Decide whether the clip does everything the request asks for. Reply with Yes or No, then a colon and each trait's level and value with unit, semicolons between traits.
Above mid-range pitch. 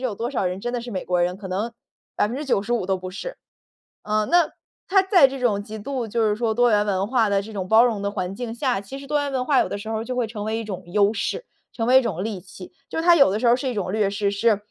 Yes: high, 220 Hz